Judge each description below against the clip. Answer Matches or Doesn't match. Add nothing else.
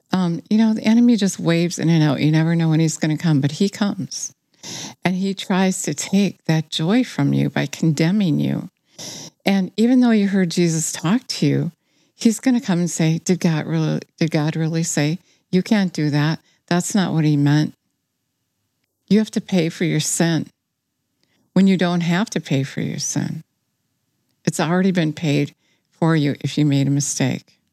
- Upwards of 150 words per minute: Matches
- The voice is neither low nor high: Matches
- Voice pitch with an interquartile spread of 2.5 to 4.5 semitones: Matches